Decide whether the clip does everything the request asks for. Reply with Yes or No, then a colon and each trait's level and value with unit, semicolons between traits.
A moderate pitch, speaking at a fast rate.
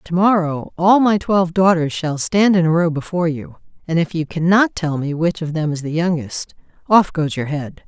Yes: medium, 170 Hz; fast, 220 wpm